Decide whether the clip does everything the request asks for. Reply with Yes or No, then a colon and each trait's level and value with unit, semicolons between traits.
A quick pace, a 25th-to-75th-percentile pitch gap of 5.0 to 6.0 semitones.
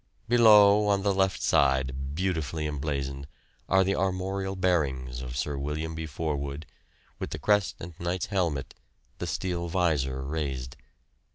No: slow, 135 wpm; wide, 5.5 semitones